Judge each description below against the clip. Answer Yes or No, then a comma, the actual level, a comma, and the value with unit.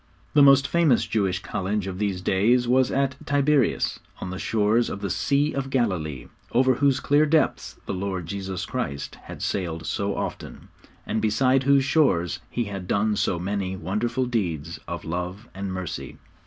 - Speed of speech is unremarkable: Yes, average, 170 wpm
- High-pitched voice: No, low, 105 Hz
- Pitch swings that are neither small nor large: No, wide, 6.0 semitones